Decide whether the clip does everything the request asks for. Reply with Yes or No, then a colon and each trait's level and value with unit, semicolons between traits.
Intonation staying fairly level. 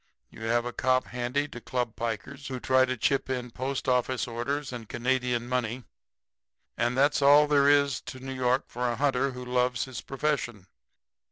Yes: narrow, 2.0 semitones